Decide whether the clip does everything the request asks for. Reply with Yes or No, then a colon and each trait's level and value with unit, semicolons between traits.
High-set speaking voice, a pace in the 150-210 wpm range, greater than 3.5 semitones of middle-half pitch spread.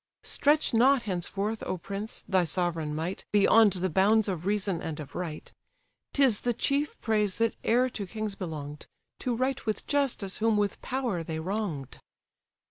Yes: high, 205 Hz; average, 160 wpm; average, 4.4 semitones